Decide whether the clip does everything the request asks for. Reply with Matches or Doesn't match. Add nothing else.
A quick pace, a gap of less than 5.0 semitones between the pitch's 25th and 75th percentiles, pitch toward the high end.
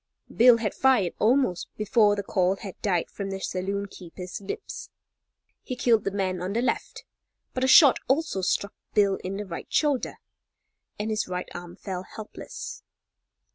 Doesn't match